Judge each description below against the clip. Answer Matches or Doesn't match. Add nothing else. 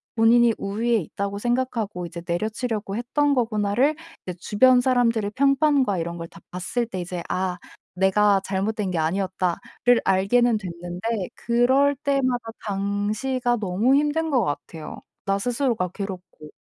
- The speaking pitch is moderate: Doesn't match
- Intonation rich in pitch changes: Doesn't match